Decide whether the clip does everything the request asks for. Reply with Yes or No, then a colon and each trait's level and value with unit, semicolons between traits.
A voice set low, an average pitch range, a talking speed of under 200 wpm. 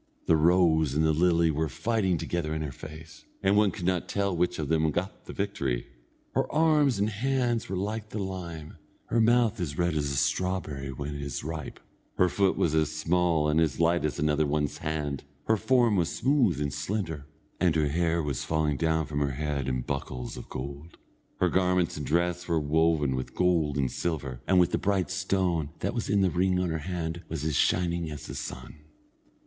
No: very low, 80 Hz; average, 3.8 semitones; fast, 205 wpm